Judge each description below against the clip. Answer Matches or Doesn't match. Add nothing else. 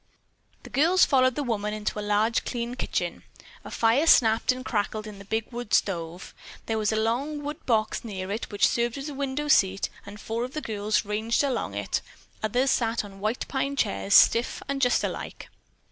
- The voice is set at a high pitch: Matches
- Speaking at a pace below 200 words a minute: Doesn't match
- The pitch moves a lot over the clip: Doesn't match